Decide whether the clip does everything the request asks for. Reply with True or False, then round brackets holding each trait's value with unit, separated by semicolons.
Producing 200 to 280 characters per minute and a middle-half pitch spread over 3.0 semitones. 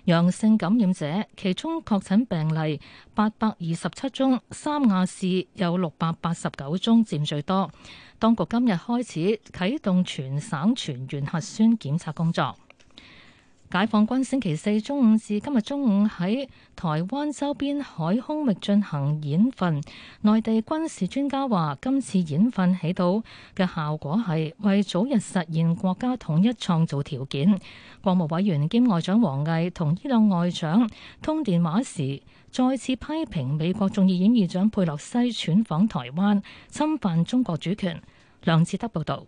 True (230 characters per minute; 5.5 semitones)